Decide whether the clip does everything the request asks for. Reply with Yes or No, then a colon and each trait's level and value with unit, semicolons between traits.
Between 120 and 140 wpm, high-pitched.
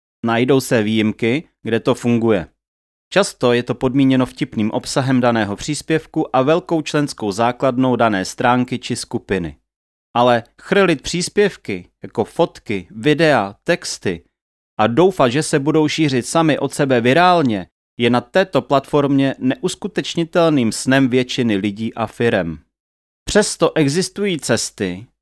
No: average, 125 wpm; low, 130 Hz